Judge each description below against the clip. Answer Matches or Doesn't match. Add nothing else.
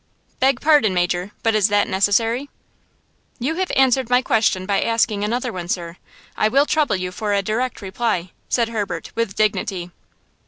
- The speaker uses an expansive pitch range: Doesn't match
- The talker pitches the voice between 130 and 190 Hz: Doesn't match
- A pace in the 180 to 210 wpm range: Doesn't match